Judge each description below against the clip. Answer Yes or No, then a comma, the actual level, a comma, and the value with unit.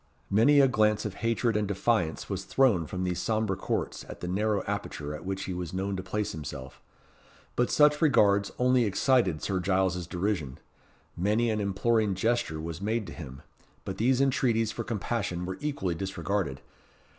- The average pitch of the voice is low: Yes, low, 100 Hz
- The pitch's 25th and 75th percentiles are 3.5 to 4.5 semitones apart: Yes, average, 4.2 semitones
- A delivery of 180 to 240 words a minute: No, average, 170 wpm